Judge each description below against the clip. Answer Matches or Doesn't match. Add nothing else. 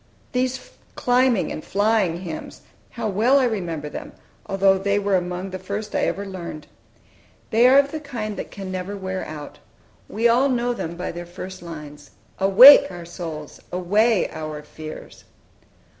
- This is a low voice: Doesn't match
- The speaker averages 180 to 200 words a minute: Doesn't match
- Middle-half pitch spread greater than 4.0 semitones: Matches